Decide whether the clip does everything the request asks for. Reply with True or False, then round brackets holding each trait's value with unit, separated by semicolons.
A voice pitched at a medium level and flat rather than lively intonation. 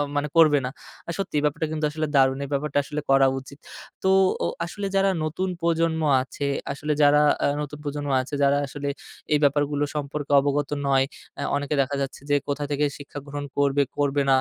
True (145 Hz; 1.3 semitones)